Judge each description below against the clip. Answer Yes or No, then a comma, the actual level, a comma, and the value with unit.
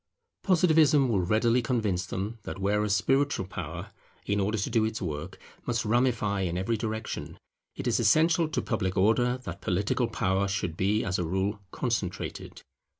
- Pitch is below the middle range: Yes, low, 110 Hz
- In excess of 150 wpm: Yes, average, 160 wpm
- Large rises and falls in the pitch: No, average, 4.2 semitones